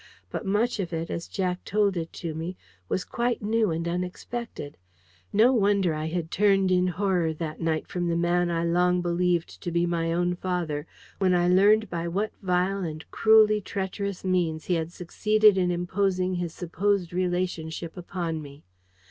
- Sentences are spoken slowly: No, average, 175 wpm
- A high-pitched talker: No, medium, 180 Hz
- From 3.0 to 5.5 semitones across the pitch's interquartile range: No, narrow, 2.6 semitones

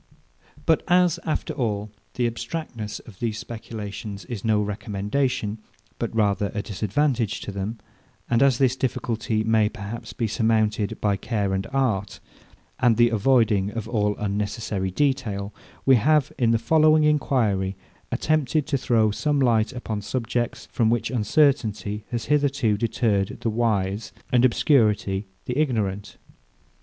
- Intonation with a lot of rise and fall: No, average, 3.7 semitones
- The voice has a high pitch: No, low, 115 Hz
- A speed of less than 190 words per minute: Yes, average, 140 wpm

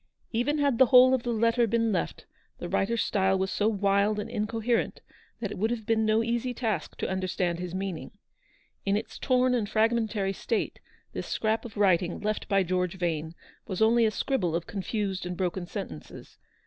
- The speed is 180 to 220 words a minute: Yes, average, 185 wpm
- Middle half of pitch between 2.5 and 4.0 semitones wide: Yes, average, 3.5 semitones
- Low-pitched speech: No, high, 210 Hz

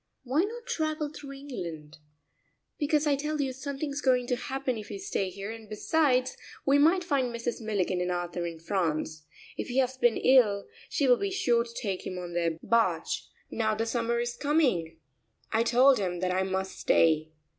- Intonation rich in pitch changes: Yes, wide, 6.9 semitones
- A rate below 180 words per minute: No, average, 190 wpm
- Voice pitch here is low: No, high, 235 Hz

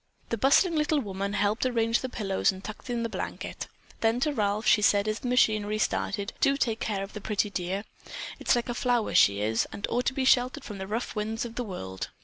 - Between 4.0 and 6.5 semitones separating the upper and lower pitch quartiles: No, average, 3.4 semitones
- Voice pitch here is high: Yes, high, 215 Hz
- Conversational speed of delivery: No, fast, 230 wpm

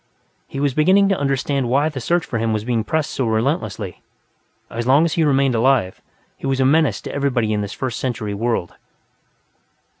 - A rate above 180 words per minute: Yes, average, 190 wpm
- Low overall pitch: Yes, low, 130 Hz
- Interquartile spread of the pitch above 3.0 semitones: Yes, average, 4.1 semitones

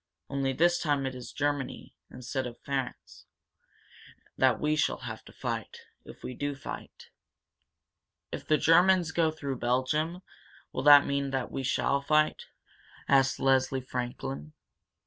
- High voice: No, medium, 140 Hz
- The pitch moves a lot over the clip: No, average, 2.8 semitones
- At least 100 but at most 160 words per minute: Yes, average, 140 wpm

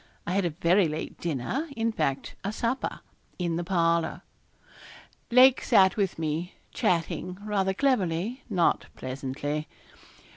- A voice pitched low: No, medium, 180 Hz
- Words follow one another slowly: Yes, slow, 125 wpm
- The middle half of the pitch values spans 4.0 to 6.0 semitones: Yes, average, 4.4 semitones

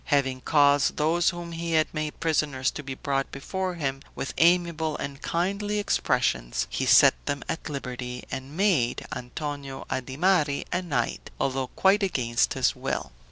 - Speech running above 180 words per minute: No, average, 155 wpm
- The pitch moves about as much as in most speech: Yes, average, 4.2 semitones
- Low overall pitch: No, medium, 145 Hz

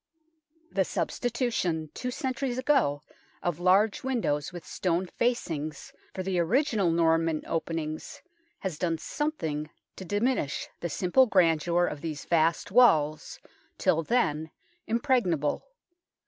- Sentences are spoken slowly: Yes, slow, 130 wpm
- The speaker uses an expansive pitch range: Yes, wide, 6.8 semitones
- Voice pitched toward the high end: No, medium, 175 Hz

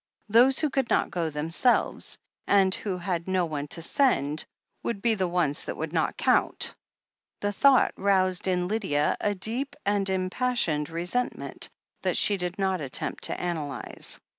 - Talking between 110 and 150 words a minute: No, average, 160 wpm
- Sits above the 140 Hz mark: Yes, medium, 185 Hz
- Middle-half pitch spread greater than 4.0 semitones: Yes, average, 4.4 semitones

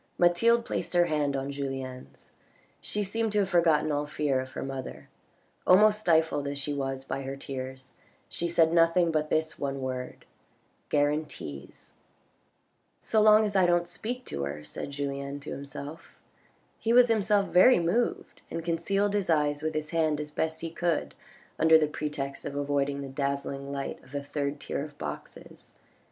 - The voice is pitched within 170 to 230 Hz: No, medium, 150 Hz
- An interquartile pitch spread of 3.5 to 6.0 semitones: Yes, average, 3.9 semitones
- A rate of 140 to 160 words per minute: No, average, 175 wpm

